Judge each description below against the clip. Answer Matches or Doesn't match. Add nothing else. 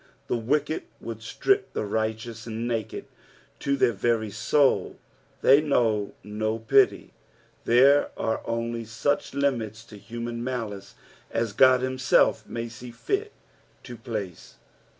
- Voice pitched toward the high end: Doesn't match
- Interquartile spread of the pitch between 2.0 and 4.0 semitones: Matches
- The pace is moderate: Doesn't match